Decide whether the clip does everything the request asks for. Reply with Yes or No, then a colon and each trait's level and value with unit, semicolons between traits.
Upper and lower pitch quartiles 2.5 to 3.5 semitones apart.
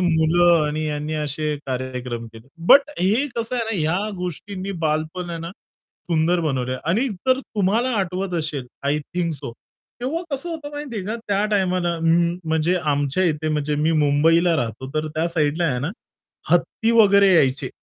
No: average, 4.3 semitones